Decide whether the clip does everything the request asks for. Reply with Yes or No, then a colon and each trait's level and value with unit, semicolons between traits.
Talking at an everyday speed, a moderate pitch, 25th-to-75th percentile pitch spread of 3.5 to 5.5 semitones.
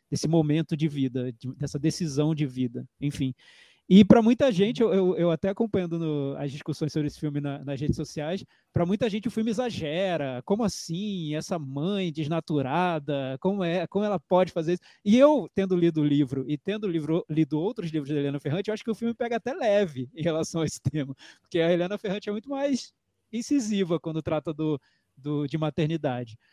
No: fast, 200 wpm; medium, 165 Hz; average, 4.9 semitones